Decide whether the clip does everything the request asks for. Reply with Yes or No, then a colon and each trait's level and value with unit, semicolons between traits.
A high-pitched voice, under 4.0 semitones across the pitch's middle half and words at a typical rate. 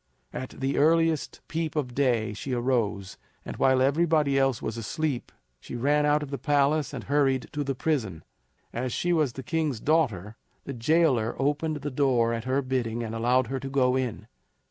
No: low, 135 Hz; average, 3.6 semitones; average, 185 wpm